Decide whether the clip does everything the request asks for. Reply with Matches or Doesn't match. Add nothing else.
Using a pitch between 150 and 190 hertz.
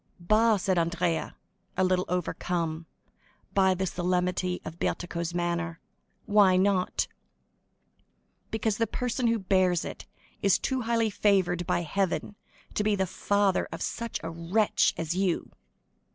Matches